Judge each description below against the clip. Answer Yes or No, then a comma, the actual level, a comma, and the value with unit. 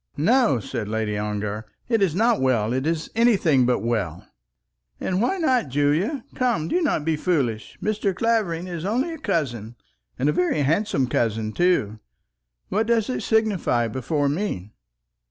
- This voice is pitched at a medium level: Yes, medium, 160 Hz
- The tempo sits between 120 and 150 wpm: No, average, 160 wpm